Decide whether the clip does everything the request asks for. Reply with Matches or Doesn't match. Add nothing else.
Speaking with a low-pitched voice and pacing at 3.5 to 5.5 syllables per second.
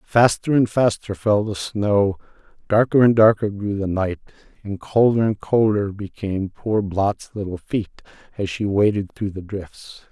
Matches